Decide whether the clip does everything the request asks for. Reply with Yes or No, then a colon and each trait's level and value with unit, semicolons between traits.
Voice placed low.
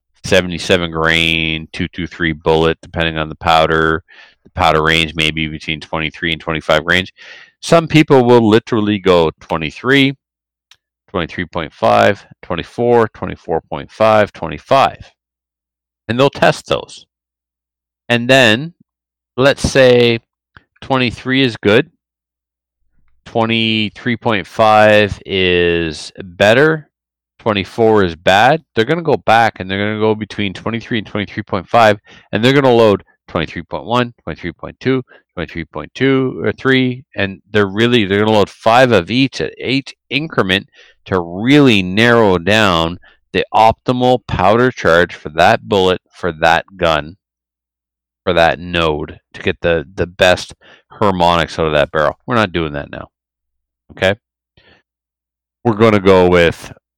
Yes: very low, 90 Hz